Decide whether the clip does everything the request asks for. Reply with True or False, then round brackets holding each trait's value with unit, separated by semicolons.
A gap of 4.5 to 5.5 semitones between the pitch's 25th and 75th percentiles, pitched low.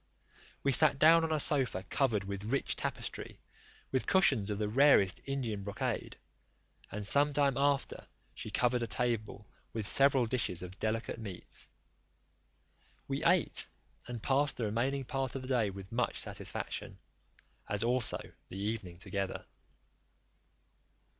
True (4.9 semitones; 120 Hz)